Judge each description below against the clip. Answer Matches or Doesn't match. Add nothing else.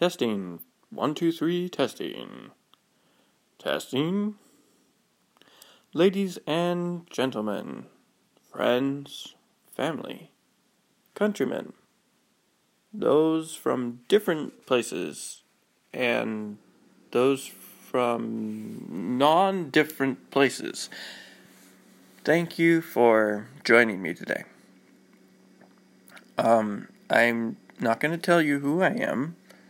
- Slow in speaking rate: Matches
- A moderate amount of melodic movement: Doesn't match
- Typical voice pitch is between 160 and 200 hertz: Doesn't match